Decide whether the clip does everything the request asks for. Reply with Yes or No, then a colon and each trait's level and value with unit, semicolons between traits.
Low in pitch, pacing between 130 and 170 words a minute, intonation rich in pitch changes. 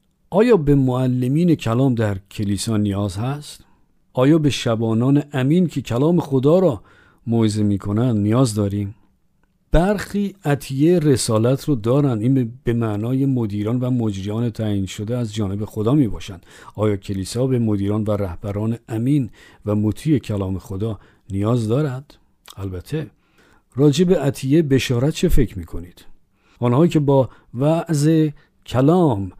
Yes: low, 120 Hz; average, 135 wpm; wide, 5.8 semitones